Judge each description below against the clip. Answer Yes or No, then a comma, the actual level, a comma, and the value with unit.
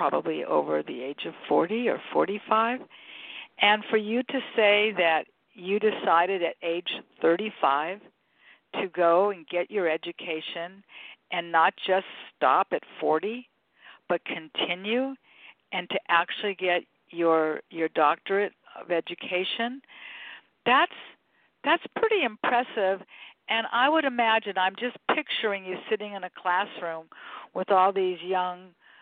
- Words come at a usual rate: No, slow, 130 wpm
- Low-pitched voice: No, high, 190 Hz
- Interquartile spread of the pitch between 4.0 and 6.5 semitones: Yes, average, 4.3 semitones